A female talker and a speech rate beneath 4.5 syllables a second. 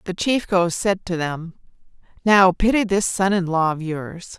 Yes: female; 4.2 syllables/s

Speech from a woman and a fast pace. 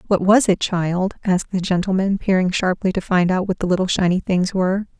Yes: female; fast, 215 wpm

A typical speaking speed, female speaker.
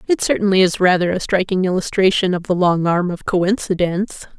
Yes: average, 180 wpm; female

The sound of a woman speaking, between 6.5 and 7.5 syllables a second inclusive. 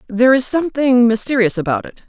Yes: female; 6.6 syllables/s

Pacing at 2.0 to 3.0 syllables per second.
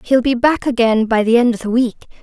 No: 5.9 syllables/s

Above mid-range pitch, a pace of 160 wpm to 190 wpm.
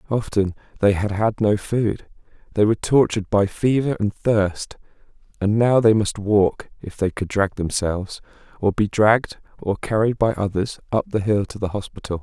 No: low, 105 Hz; average, 175 wpm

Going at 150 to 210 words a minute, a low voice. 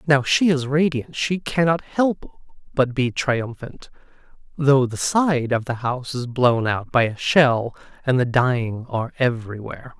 Yes: average, 160 wpm; low, 130 Hz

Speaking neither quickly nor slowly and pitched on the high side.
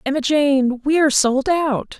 Yes: average, 180 wpm; very high, 275 Hz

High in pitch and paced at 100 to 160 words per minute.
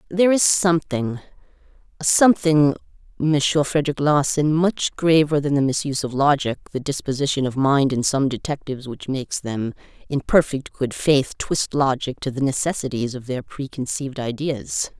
No: medium, 140 Hz; average, 150 wpm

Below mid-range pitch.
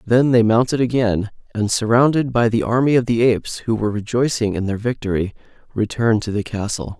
Yes: low, 115 Hz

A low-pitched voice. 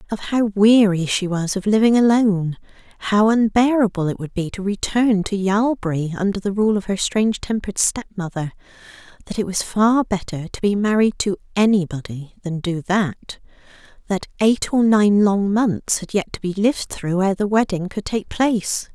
No: high, 200 Hz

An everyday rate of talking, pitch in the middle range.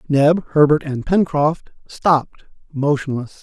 No: slow, 105 wpm; medium, 150 Hz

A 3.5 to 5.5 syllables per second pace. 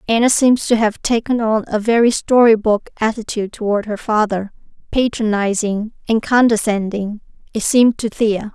Yes: 5.2 syllables/s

